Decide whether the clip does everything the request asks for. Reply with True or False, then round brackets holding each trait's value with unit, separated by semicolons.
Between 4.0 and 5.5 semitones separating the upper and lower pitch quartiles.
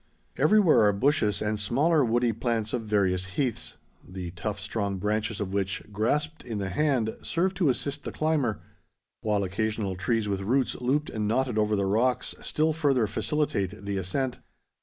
True (5.2 semitones)